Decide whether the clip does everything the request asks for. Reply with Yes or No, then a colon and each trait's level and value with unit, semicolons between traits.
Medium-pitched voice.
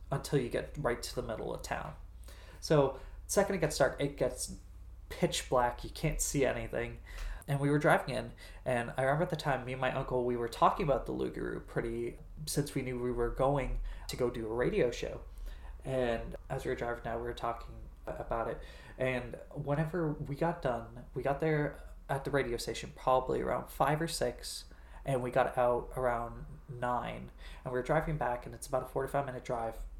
No: low, 125 Hz